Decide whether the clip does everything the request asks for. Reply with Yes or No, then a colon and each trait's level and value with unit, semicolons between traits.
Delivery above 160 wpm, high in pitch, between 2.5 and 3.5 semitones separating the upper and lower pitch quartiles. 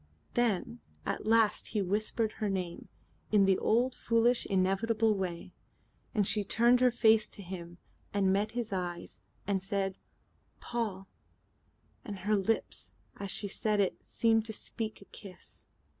No: average, 150 wpm; high, 210 Hz; average, 2.8 semitones